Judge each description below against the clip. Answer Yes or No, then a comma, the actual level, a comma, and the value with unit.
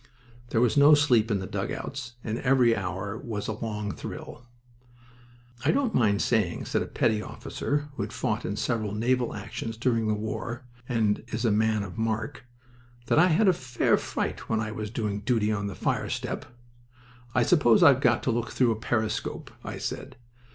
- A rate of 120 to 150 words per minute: No, average, 185 wpm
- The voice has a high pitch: No, low, 115 Hz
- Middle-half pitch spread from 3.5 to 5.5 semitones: No, average, 2.8 semitones